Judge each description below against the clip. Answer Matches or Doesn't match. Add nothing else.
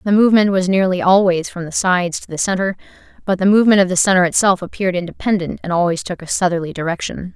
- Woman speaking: Matches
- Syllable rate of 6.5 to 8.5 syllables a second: Matches